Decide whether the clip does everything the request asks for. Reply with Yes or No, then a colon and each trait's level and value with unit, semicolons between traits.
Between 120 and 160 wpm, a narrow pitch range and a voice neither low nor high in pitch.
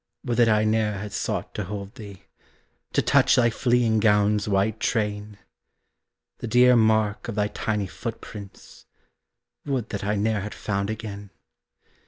No: average, 150 wpm; narrow, 1.5 semitones; low, 105 Hz